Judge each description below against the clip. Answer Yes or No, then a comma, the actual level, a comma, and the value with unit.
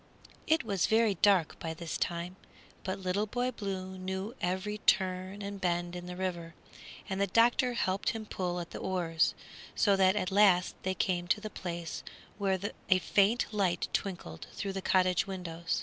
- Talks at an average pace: Yes, average, 175 wpm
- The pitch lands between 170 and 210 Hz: Yes, high, 190 Hz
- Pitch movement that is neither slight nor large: No, narrow, 2.2 semitones